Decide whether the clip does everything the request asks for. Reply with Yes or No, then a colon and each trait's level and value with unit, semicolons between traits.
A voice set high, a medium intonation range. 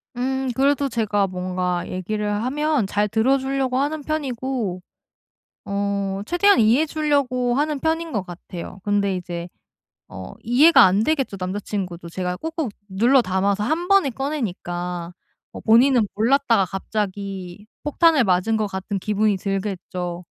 No: high, 215 Hz; wide, 6.2 semitones